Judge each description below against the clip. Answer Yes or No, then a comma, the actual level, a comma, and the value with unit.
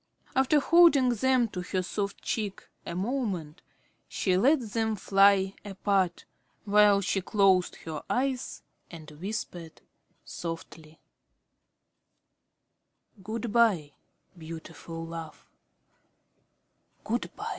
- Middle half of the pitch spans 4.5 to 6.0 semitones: Yes, average, 5.1 semitones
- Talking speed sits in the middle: No, slow, 95 wpm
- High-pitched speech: Yes, high, 195 Hz